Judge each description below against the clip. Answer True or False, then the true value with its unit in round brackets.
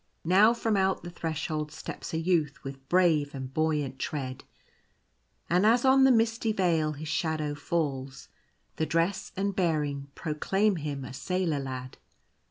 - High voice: False (160 Hz)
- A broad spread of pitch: False (4.6 semitones)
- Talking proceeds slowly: False (150 wpm)